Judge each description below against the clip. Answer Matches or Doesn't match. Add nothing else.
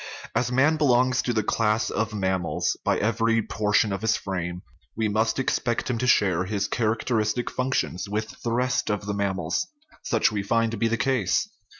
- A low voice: Matches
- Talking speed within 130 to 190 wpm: Doesn't match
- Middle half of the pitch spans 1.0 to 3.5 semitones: Matches